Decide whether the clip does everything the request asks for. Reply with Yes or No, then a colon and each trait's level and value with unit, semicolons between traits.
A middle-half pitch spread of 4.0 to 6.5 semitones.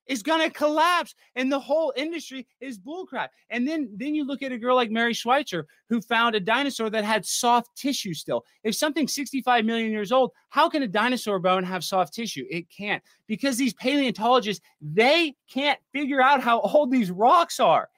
Yes: average, 4.3 semitones